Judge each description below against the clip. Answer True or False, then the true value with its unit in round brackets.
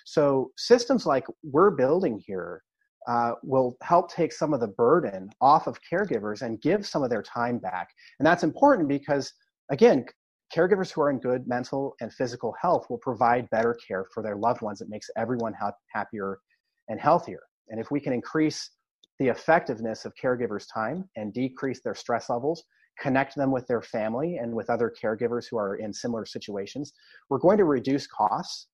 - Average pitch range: True (4.5 semitones)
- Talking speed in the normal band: True (180 wpm)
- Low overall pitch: True (130 Hz)